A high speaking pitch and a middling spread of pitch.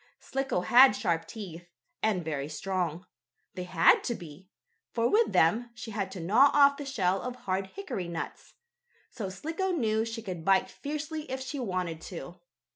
No: high, 200 Hz; wide, 6.7 semitones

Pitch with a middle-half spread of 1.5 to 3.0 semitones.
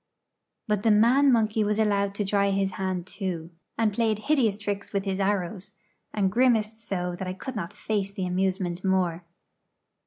Yes: narrow, 2.4 semitones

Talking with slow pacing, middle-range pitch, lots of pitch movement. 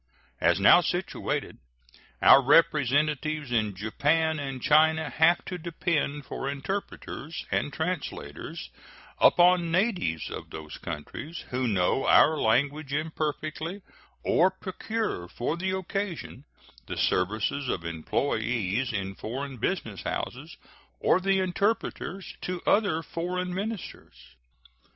Yes: slow, 110 wpm; medium, 155 Hz; wide, 6.4 semitones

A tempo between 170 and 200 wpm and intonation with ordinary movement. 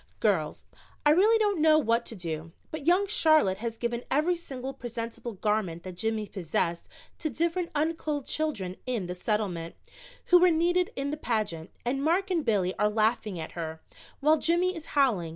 No: average, 175 wpm; wide, 8.1 semitones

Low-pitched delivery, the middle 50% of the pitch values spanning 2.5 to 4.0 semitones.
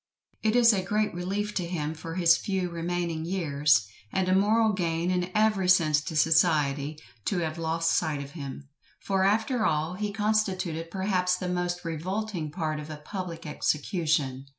No: medium, 175 Hz; average, 3.4 semitones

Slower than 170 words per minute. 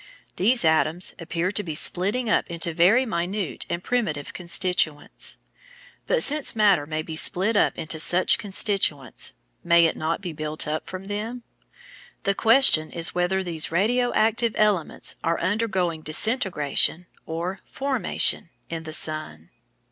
Yes: average, 140 wpm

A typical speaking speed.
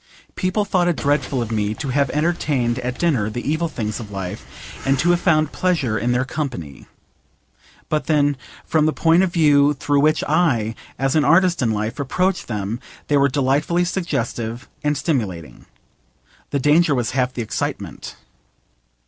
Yes: average, 165 wpm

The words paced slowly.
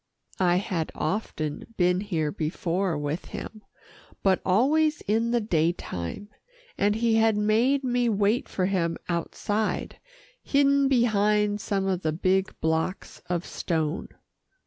Yes: slow, 125 wpm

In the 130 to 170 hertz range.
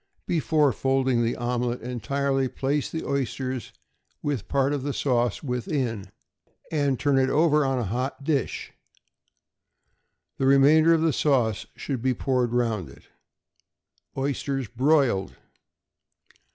Yes: low, 135 Hz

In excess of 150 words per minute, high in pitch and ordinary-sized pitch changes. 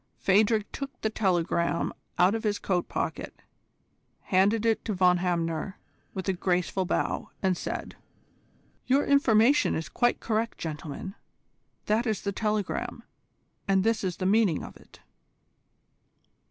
No: slow, 135 wpm; high, 195 Hz; average, 3.6 semitones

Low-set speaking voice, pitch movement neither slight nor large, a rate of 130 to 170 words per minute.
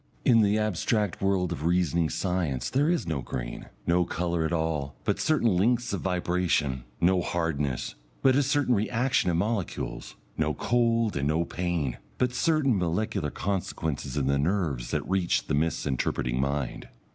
No: very low, 90 Hz; wide, 6.5 semitones; average, 155 wpm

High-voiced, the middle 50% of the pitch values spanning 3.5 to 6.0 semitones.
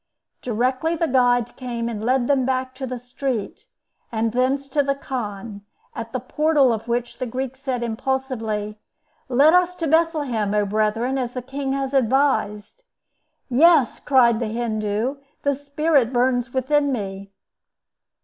No: very high, 255 Hz; average, 3.1 semitones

